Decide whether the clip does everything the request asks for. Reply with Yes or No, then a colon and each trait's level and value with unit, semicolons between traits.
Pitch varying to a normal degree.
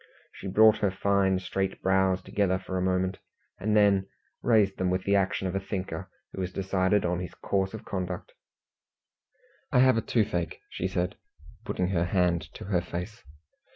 No: narrow, 1.4 semitones